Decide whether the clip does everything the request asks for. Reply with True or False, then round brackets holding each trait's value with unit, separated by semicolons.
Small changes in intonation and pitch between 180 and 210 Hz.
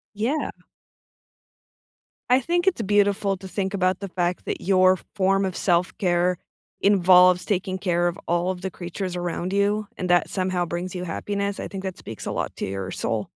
True (2.0 semitones; 185 Hz)